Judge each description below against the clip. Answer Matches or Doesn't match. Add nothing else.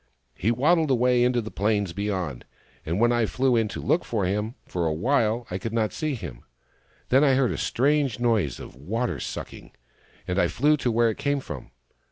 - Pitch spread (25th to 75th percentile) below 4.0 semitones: Doesn't match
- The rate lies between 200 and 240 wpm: Matches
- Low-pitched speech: Matches